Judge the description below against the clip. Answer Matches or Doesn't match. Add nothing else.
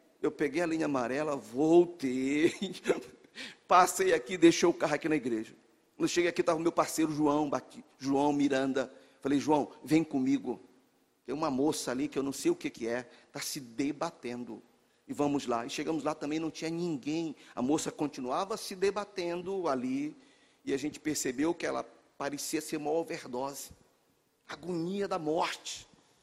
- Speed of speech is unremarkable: Matches